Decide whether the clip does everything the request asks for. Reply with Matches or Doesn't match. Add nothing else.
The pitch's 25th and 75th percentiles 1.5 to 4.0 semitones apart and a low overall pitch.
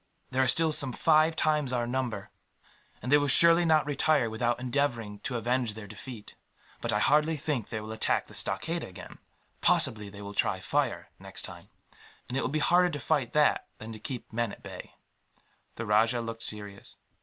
Doesn't match